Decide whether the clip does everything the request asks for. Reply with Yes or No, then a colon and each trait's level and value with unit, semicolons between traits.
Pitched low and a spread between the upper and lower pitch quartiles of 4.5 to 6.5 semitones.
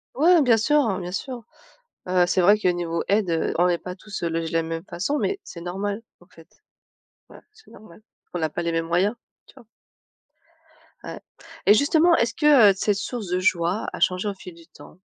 No: high, 190 Hz; average, 4.8 semitones